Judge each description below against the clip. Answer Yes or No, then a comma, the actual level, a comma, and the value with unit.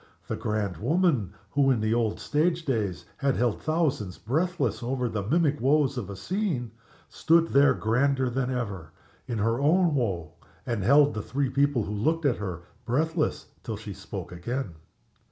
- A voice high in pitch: No, low, 125 Hz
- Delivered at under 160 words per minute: No, average, 170 wpm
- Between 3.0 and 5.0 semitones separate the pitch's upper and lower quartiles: No, wide, 5.5 semitones